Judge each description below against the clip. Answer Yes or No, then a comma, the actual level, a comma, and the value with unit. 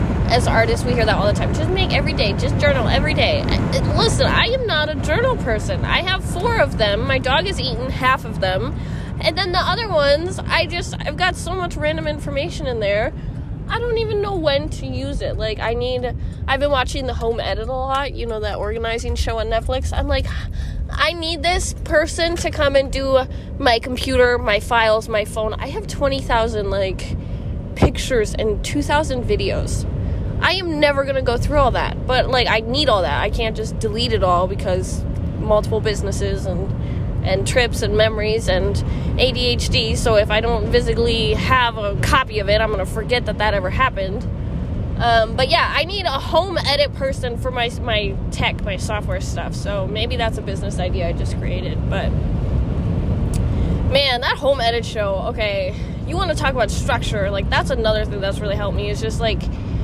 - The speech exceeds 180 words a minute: Yes, average, 200 wpm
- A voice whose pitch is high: Yes, very high, 260 Hz